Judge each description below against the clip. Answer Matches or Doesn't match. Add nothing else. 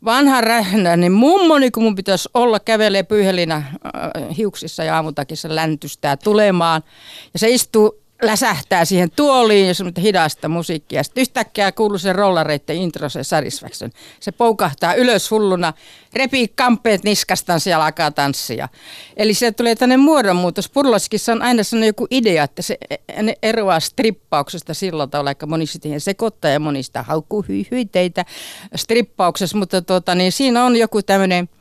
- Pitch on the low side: Doesn't match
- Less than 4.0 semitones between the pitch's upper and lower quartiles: Doesn't match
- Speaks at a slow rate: Doesn't match